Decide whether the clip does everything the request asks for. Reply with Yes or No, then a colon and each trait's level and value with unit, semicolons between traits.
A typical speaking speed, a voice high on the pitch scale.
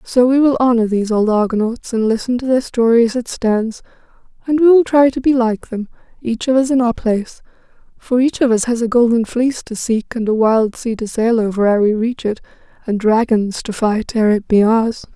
No: fast, 230 wpm; high, 230 Hz